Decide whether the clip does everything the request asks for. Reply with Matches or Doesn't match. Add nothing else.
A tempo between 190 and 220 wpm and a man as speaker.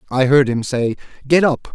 Matches